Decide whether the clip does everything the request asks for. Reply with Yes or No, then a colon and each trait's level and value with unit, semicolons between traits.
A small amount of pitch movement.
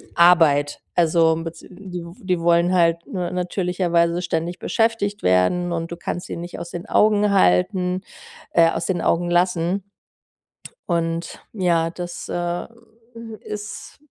Yes: narrow, 1.5 semitones